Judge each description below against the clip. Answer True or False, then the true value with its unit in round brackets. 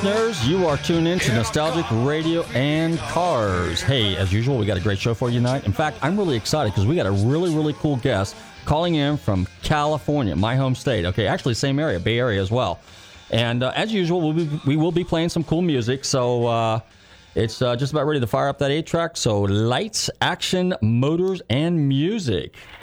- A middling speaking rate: False (215 wpm)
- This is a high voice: False (135 Hz)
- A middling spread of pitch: False (6.1 semitones)